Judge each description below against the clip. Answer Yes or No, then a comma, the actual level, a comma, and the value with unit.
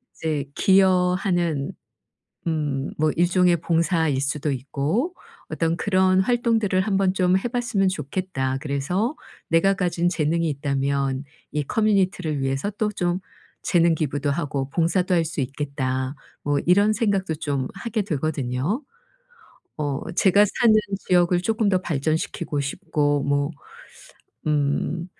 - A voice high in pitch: No, medium, 170 Hz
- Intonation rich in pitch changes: No, average, 4.8 semitones